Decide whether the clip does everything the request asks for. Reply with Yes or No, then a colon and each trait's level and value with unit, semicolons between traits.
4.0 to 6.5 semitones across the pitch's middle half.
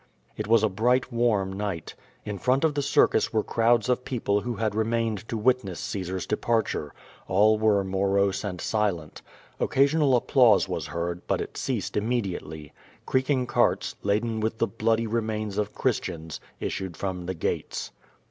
No: average, 3.5 semitones